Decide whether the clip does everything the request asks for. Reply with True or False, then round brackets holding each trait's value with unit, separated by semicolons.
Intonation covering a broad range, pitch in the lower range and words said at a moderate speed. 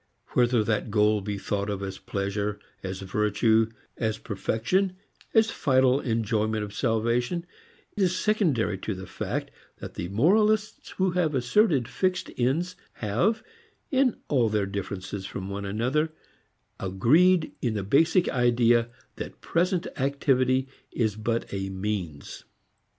False (7.2 semitones; 115 Hz; 130 wpm)